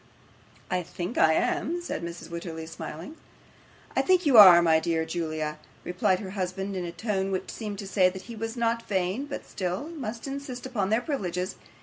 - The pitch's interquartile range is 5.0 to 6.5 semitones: Yes, average, 5.3 semitones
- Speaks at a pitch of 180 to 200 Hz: Yes, high, 190 Hz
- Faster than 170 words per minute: Yes, average, 190 wpm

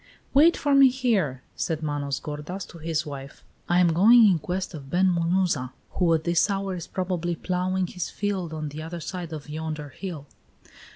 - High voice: No, medium, 170 Hz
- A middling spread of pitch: Yes, average, 3.5 semitones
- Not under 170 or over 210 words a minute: Yes, average, 185 wpm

